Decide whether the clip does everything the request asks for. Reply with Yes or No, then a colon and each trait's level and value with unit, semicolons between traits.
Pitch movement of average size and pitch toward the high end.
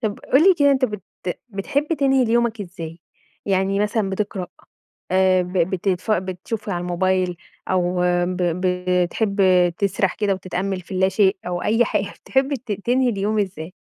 Yes: average, 3.2 semitones; high, 195 Hz